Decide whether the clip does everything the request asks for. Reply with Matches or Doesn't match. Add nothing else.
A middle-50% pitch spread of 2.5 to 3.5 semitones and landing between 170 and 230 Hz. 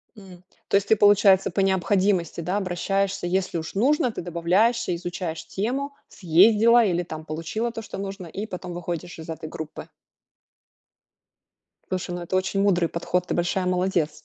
Matches